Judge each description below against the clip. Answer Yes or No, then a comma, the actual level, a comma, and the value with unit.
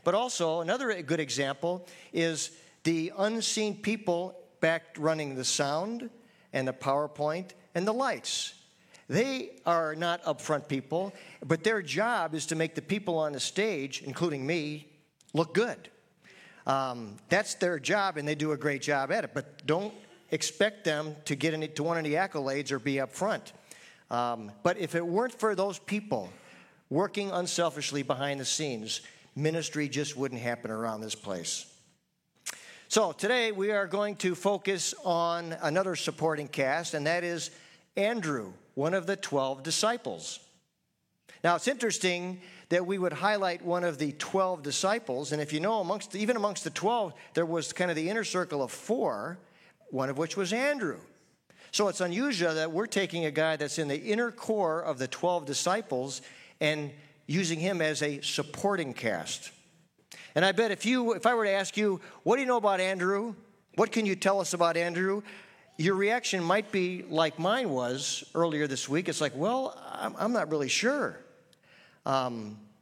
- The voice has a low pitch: No, medium, 170 Hz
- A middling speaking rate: Yes, average, 170 wpm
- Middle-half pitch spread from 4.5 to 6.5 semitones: Yes, average, 4.8 semitones